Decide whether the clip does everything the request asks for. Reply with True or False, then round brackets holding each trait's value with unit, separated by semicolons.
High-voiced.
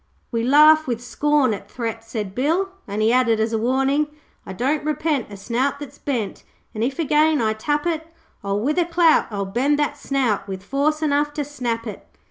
True (265 Hz)